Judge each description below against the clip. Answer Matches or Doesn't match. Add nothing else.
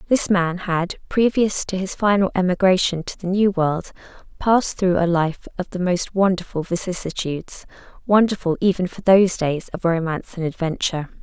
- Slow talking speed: Doesn't match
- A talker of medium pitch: Matches